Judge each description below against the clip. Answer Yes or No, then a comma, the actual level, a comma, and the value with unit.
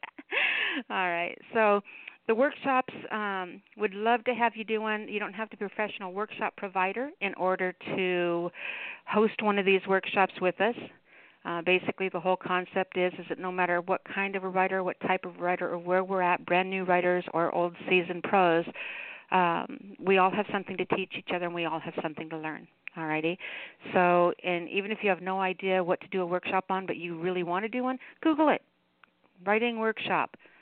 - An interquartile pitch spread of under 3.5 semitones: Yes, average, 2.9 semitones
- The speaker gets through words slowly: No, average, 200 wpm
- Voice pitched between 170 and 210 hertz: Yes, medium, 185 Hz